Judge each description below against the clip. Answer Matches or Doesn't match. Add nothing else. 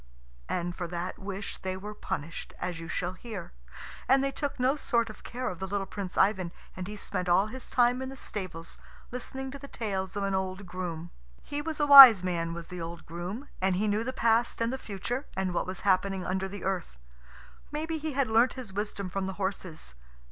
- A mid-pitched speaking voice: Doesn't match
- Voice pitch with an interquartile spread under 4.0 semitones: Doesn't match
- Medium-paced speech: Doesn't match